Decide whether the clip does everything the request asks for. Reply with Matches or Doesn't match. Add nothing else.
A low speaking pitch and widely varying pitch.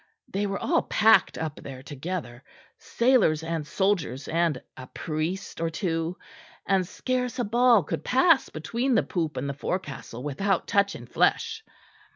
Doesn't match